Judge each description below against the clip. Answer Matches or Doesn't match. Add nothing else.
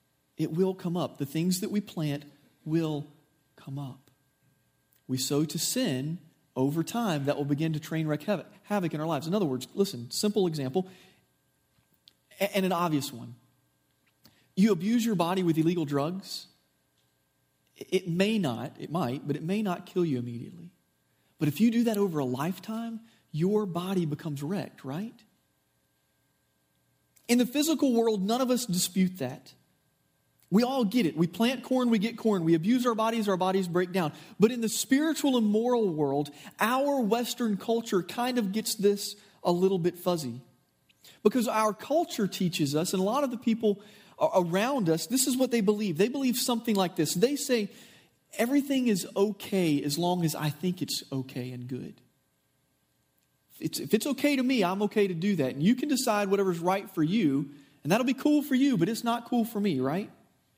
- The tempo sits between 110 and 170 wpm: Doesn't match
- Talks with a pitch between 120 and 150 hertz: Doesn't match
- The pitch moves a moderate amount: Doesn't match